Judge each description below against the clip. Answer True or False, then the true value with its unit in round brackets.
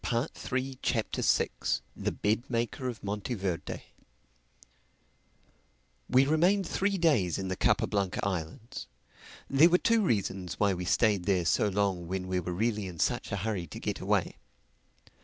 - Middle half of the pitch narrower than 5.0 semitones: False (5.6 semitones)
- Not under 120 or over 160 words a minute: True (150 wpm)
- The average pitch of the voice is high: False (105 Hz)